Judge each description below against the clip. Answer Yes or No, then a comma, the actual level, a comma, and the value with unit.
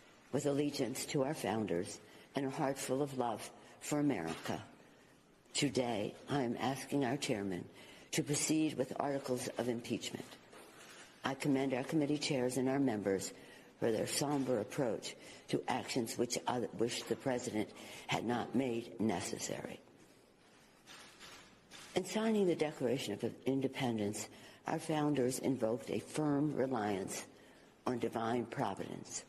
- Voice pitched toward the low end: Yes, low, 130 Hz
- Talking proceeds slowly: Yes, slow, 130 wpm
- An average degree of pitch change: Yes, average, 3.9 semitones